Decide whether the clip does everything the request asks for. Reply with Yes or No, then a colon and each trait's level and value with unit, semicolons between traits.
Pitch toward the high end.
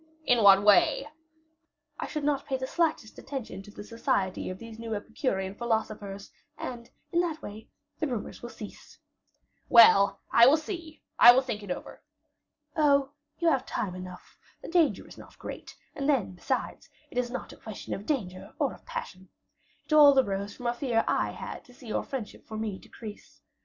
Yes: high, 235 Hz